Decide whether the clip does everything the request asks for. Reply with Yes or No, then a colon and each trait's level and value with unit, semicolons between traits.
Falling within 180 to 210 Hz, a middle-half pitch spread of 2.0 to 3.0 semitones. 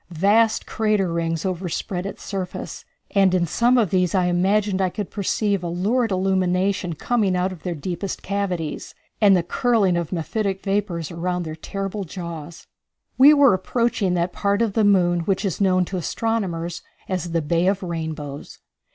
Yes: medium, 185 Hz; average, 2.7 semitones